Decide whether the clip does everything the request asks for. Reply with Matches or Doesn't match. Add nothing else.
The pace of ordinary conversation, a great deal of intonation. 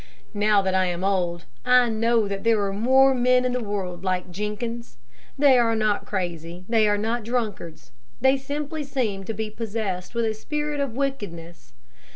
Doesn't match